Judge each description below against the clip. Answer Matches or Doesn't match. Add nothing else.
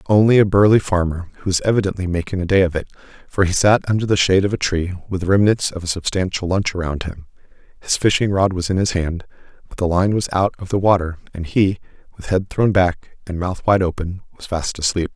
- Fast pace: Matches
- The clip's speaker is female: Doesn't match